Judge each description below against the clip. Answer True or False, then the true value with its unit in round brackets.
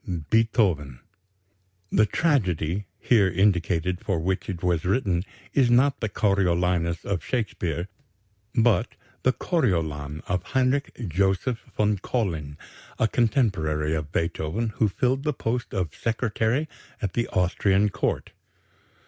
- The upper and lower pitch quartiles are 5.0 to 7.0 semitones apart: True (5.3 semitones)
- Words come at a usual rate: False (120 wpm)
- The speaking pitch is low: True (95 Hz)